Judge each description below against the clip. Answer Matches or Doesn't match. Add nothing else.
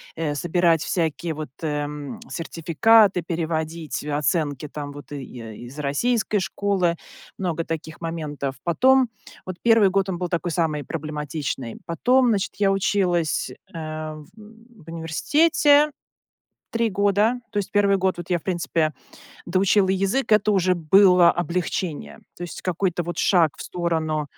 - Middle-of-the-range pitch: Matches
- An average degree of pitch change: Matches